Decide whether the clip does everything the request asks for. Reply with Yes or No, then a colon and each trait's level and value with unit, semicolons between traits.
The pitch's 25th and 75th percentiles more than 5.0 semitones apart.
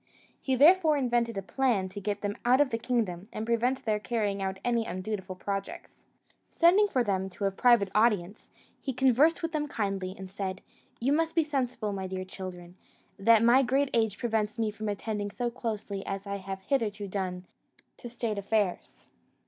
No: average, 4.1 semitones